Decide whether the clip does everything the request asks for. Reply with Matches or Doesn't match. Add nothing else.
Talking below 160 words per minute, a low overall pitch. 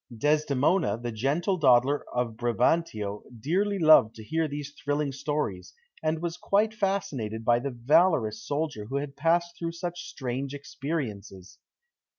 Doesn't match